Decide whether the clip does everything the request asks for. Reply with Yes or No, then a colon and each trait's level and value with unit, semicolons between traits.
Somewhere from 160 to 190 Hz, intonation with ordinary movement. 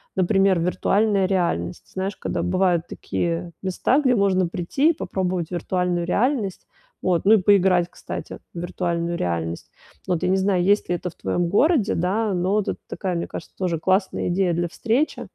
No: medium, 185 Hz; narrow, 2.3 semitones